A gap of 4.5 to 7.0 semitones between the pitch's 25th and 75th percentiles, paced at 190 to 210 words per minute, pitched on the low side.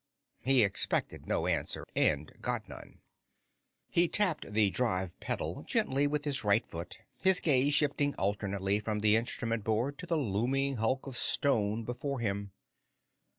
No: wide, 5.5 semitones; average, 150 wpm; low, 115 Hz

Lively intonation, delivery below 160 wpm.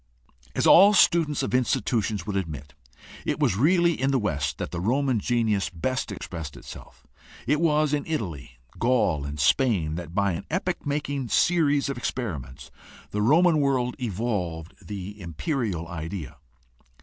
Yes: wide, 8.8 semitones; average, 150 wpm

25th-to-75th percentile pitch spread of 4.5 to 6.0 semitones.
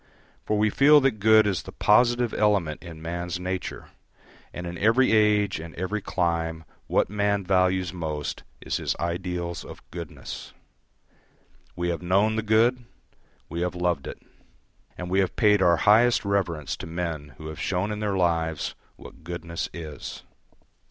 No: average, 3.7 semitones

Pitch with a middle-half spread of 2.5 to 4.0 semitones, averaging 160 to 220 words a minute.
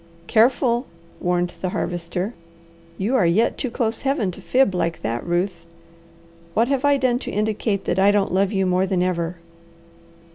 No: average, 4.9 semitones; average, 170 wpm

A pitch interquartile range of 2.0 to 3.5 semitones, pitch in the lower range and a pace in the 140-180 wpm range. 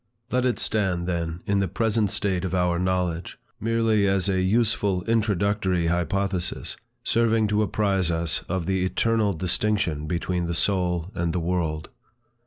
Yes: average, 3.2 semitones; very low, 95 Hz; average, 150 wpm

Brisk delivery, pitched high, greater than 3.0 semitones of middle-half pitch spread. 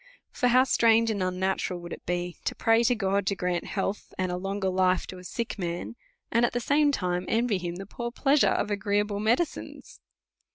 Yes: fast, 215 wpm; high, 200 Hz; average, 4.1 semitones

